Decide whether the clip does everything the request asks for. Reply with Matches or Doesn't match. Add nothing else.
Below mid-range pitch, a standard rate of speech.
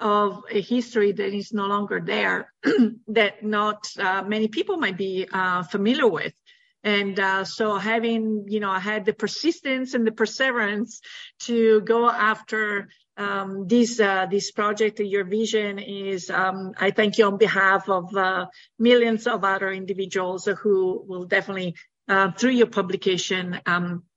Doesn't match